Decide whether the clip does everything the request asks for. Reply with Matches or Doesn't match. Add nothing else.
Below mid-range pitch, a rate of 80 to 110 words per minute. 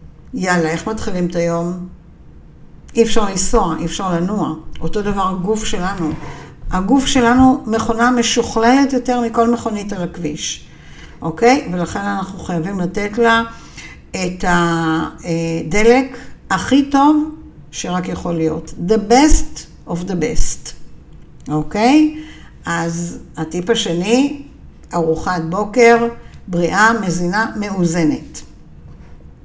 Doesn't match